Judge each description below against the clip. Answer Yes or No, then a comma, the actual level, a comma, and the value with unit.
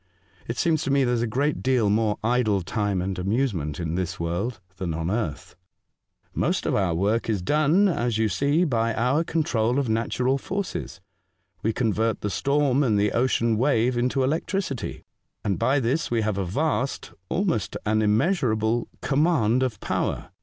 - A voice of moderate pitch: No, low, 115 Hz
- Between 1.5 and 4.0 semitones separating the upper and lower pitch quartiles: No, average, 4.8 semitones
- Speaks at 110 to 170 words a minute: No, average, 180 wpm